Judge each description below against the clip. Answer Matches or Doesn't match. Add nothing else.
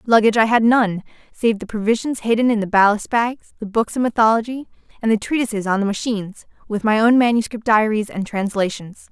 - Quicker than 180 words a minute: Matches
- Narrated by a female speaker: Matches